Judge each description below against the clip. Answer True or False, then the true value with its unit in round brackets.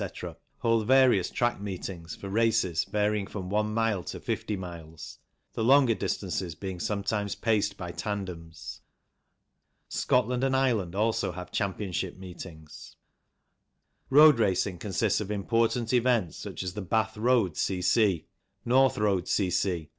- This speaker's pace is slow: True (130 wpm)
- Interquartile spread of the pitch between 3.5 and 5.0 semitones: True (3.9 semitones)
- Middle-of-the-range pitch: False (100 Hz)